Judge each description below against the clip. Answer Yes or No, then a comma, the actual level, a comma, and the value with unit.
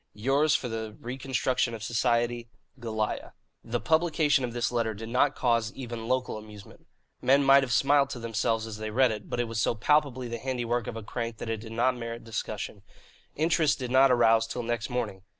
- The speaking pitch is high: No, low, 120 Hz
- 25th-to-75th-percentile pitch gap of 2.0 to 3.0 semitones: Yes, narrow, 2.5 semitones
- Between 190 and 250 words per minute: Yes, average, 200 wpm